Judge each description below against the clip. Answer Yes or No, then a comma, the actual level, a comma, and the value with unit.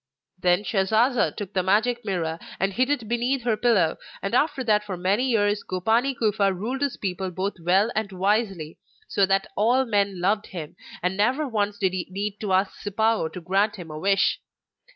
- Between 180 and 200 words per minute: Yes, average, 190 wpm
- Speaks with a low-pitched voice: No, high, 205 Hz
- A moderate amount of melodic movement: Yes, average, 3.3 semitones